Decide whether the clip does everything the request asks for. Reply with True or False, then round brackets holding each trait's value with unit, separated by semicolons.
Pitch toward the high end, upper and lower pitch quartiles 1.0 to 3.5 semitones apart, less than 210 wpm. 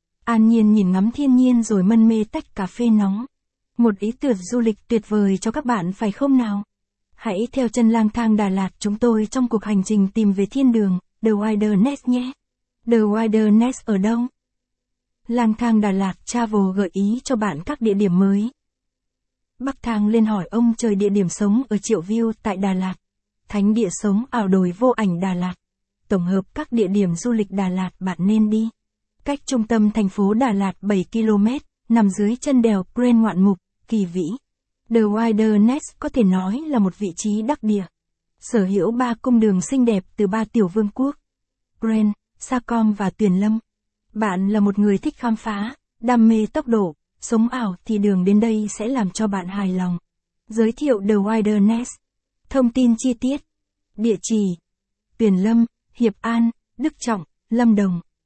True (215 Hz; 2.7 semitones; 195 wpm)